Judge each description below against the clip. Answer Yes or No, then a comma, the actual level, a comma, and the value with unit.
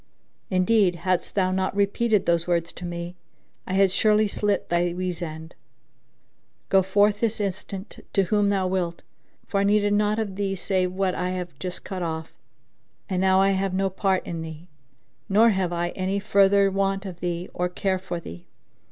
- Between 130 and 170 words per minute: No, average, 180 wpm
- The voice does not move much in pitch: Yes, narrow, 2.1 semitones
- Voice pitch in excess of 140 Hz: Yes, high, 190 Hz